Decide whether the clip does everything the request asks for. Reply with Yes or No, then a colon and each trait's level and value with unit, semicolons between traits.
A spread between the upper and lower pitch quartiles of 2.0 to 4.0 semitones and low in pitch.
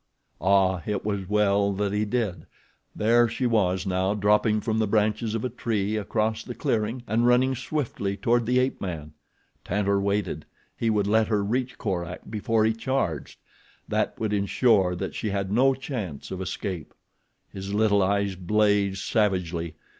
Yes: narrow, 2.6 semitones; low, 105 Hz